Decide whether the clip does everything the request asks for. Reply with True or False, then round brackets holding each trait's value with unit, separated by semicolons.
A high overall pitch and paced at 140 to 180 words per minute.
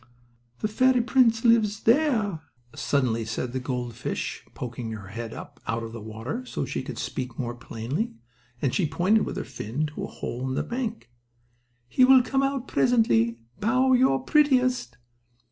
False (160 Hz; 175 wpm)